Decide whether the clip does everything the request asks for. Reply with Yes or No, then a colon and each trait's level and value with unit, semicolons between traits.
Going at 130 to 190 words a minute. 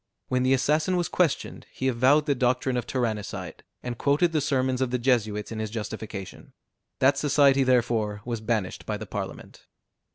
Yes: average, 170 wpm